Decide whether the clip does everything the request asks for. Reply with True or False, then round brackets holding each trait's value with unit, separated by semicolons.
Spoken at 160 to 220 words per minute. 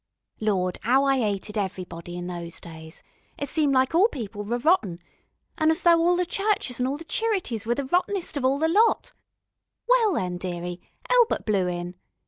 True (185 wpm)